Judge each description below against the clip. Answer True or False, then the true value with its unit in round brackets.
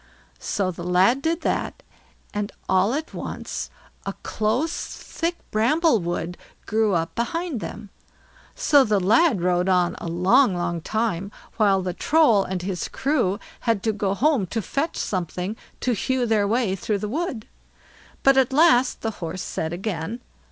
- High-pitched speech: True (215 Hz)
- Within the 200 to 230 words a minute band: False (160 wpm)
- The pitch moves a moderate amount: False (5.8 semitones)